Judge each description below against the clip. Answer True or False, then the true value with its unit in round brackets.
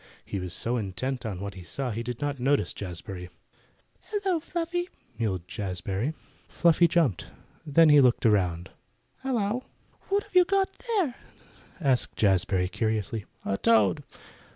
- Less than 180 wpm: True (140 wpm)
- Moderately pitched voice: False (120 Hz)